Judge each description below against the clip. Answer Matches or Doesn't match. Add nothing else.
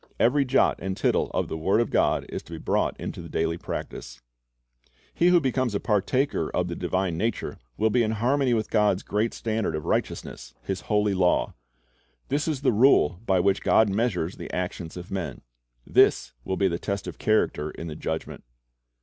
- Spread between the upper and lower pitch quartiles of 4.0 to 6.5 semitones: Matches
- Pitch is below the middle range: Matches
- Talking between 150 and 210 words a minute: Matches